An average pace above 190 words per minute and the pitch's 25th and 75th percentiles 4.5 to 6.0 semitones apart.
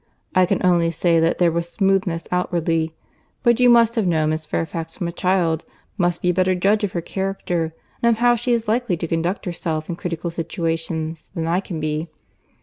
No: fast, 205 wpm; average, 2.8 semitones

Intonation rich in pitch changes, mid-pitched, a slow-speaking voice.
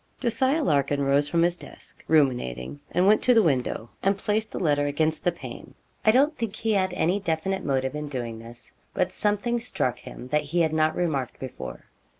No: wide, 6.5 semitones; medium, 160 Hz; average, 195 wpm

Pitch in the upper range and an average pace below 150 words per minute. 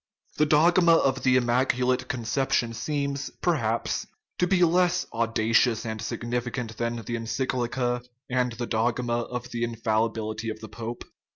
No: low, 120 Hz; slow, 135 wpm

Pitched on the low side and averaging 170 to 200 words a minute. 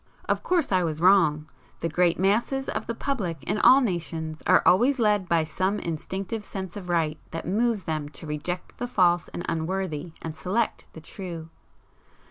No: medium, 180 Hz; average, 185 wpm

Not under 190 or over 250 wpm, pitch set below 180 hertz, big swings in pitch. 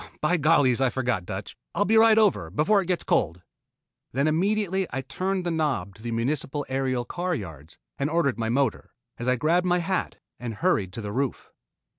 Yes: average, 195 wpm; medium, 140 Hz; wide, 7.2 semitones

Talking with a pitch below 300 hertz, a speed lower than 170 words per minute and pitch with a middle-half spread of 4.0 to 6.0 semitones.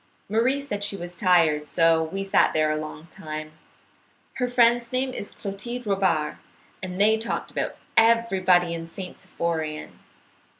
Yes: high, 190 Hz; average, 140 wpm; wide, 5.6 semitones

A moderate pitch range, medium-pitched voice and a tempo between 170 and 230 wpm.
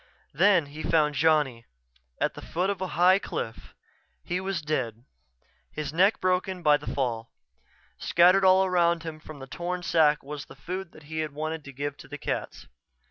Yes: average, 3.8 semitones; medium, 160 Hz; average, 180 wpm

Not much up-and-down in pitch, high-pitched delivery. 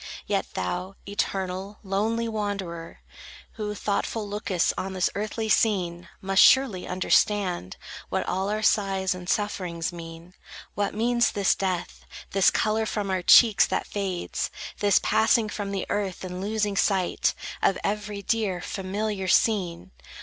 Yes: narrow, 2.3 semitones; high, 195 Hz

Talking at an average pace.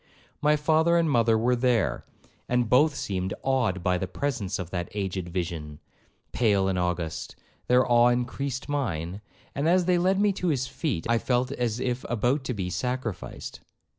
Yes: average, 170 wpm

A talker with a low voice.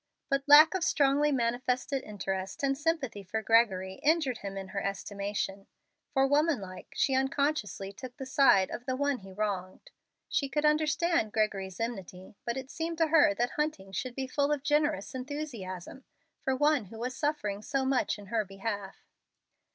No: very high, 255 Hz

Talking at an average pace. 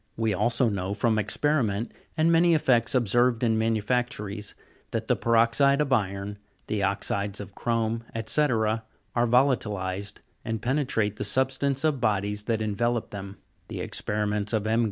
Yes: average, 150 wpm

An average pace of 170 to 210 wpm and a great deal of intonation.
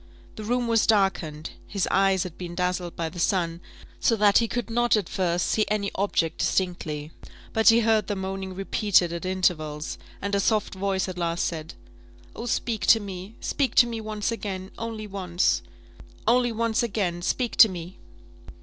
No: average, 175 wpm; average, 3.8 semitones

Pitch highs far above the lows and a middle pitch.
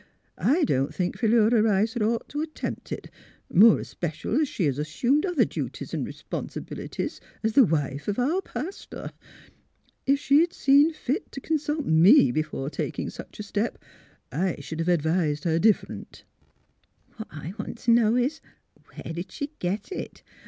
No: wide, 9.0 semitones; high, 220 Hz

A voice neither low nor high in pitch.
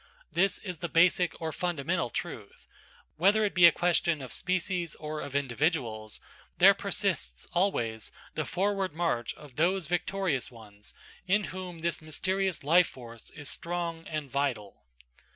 Yes: medium, 165 Hz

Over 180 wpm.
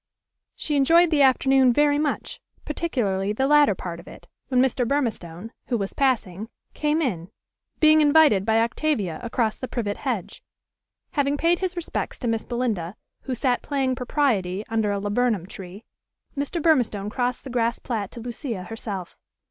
No: average, 160 wpm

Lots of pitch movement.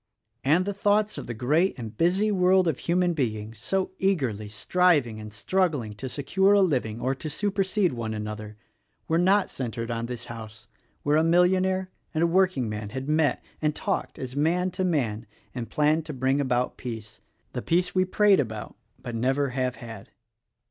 Yes: wide, 7.7 semitones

